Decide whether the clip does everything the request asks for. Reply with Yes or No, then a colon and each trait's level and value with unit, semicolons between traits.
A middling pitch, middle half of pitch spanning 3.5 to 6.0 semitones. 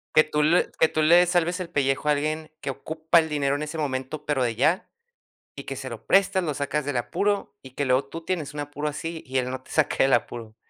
No: medium, 150 Hz; average, 3.1 semitones